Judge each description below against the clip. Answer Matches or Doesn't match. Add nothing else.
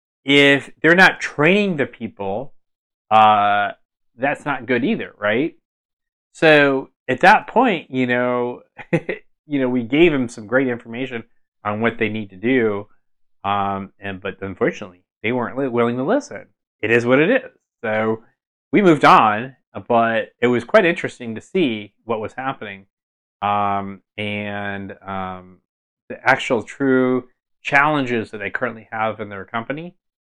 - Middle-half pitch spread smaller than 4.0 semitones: Doesn't match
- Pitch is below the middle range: Matches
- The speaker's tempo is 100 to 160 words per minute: Matches